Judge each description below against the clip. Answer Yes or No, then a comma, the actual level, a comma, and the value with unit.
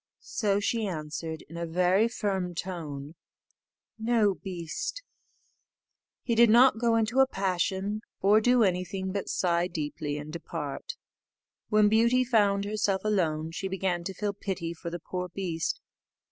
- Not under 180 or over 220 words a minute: No, average, 145 wpm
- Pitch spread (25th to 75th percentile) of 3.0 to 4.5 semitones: Yes, average, 3.9 semitones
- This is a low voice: No, high, 190 Hz